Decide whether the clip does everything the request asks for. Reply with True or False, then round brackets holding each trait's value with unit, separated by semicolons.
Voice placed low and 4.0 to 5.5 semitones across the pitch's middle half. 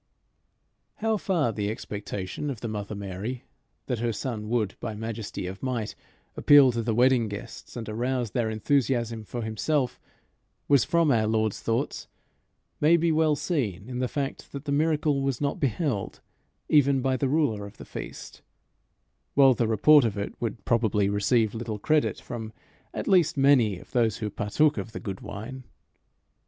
True (120 Hz; 4.5 semitones)